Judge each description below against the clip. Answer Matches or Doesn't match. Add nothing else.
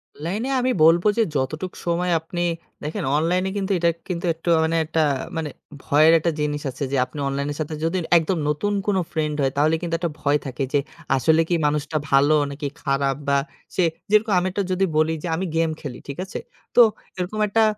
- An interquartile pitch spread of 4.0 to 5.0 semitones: Doesn't match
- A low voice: Doesn't match